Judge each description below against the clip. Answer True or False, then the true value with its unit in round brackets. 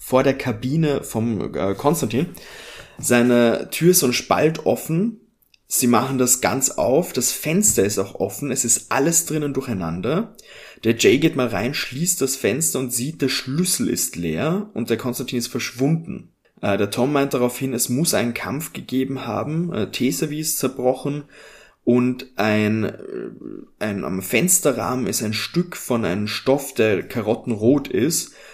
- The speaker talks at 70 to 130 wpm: False (160 wpm)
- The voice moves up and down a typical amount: True (4.0 semitones)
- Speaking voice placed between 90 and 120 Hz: False (130 Hz)